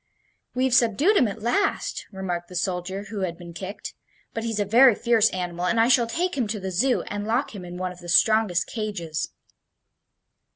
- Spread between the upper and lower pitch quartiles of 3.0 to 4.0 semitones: No, average, 4.5 semitones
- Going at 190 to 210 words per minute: Yes, average, 200 wpm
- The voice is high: Yes, high, 205 Hz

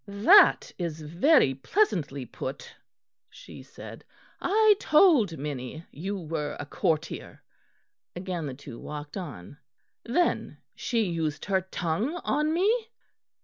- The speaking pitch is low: No, medium, 175 Hz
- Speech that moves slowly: Yes, slow, 115 wpm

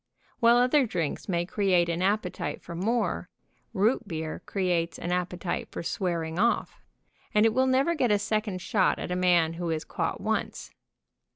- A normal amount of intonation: Yes, average, 4.4 semitones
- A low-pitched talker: No, medium, 185 Hz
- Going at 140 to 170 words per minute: No, average, 180 wpm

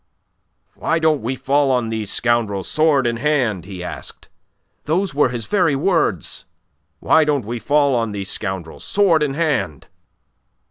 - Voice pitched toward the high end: No, low, 130 Hz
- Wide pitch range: Yes, wide, 6.0 semitones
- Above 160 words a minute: No, average, 150 wpm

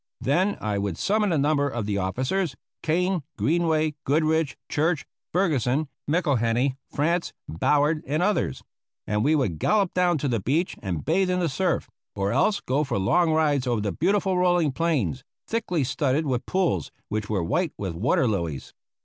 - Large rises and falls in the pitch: Yes, wide, 6.6 semitones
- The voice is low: No, medium, 150 Hz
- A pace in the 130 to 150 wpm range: No, average, 165 wpm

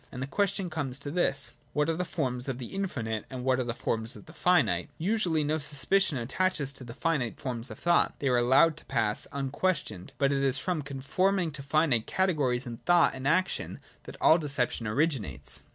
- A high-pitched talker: No, medium, 140 Hz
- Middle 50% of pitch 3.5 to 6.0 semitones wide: Yes, average, 5.0 semitones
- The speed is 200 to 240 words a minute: Yes, fast, 205 wpm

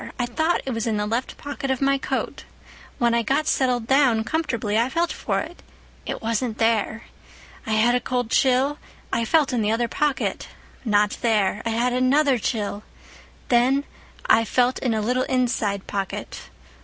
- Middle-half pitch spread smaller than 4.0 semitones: Yes, average, 3.1 semitones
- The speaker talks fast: No, average, 175 wpm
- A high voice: Yes, high, 245 Hz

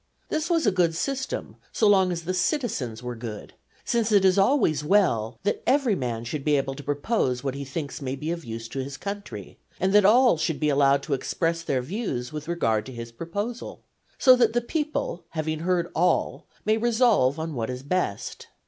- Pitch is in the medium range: Yes, medium, 165 Hz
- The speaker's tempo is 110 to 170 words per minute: No, average, 200 wpm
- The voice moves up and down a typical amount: No, wide, 7.4 semitones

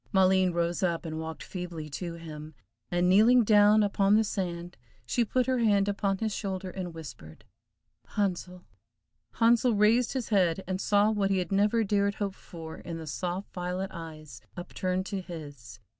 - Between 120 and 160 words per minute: No, average, 170 wpm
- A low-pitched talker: No, medium, 185 Hz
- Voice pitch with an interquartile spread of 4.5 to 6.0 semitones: No, average, 3.2 semitones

